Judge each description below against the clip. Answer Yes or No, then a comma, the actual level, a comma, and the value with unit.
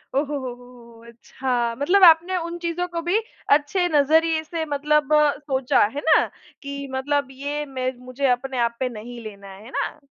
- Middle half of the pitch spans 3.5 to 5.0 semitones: Yes, average, 4.3 semitones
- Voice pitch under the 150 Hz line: No, very high, 280 Hz